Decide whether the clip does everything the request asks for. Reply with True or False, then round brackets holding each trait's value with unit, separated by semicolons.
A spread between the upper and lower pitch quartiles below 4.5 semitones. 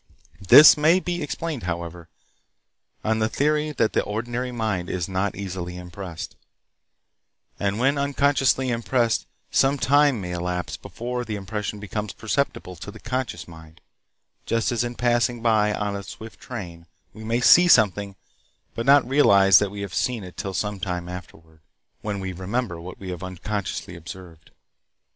False (5.2 semitones)